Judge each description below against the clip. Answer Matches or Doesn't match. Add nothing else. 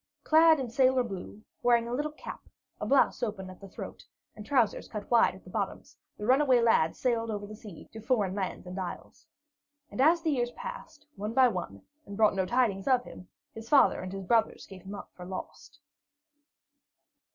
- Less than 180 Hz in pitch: Doesn't match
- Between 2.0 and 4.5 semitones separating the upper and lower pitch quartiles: Doesn't match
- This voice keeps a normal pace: Matches